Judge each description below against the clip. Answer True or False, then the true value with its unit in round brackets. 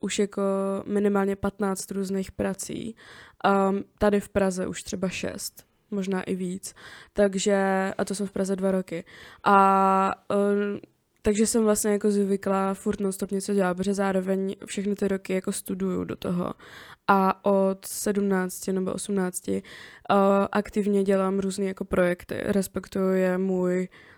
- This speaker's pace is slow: False (140 wpm)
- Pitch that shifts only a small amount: True (1.1 semitones)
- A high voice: True (195 Hz)